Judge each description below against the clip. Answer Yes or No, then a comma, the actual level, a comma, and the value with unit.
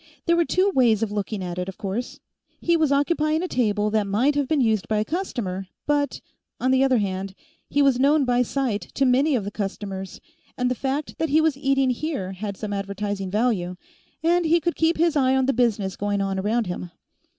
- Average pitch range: No, wide, 6.1 semitones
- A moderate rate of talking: No, fast, 215 wpm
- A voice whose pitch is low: No, high, 245 Hz